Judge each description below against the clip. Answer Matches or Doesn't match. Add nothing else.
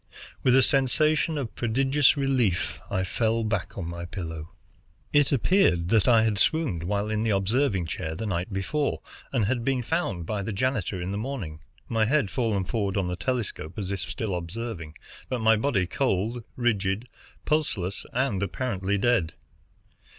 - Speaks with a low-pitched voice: Matches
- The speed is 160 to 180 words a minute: Matches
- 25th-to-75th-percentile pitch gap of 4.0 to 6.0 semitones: Matches